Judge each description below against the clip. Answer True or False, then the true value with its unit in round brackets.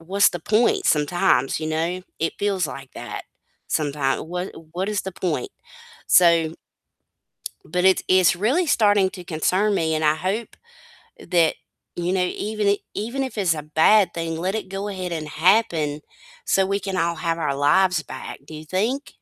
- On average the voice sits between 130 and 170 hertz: False (180 Hz)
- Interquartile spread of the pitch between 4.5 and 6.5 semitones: False (3.8 semitones)